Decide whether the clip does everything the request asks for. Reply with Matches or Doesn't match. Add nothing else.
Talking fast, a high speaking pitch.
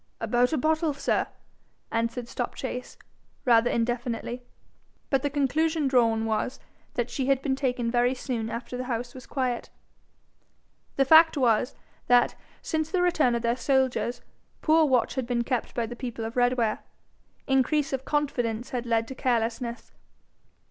Doesn't match